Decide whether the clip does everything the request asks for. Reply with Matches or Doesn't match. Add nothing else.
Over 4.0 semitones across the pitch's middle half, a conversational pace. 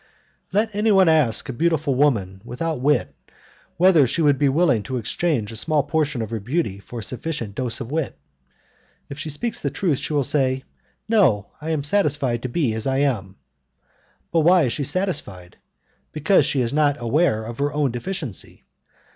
Matches